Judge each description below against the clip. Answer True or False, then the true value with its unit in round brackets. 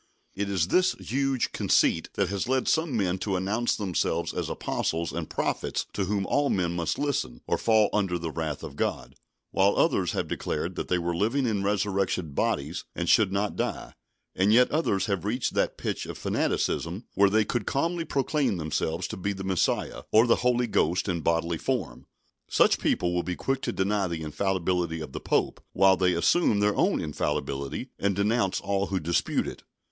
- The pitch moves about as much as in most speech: True (4.3 semitones)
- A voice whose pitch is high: False (95 Hz)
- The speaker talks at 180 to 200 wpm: True (190 wpm)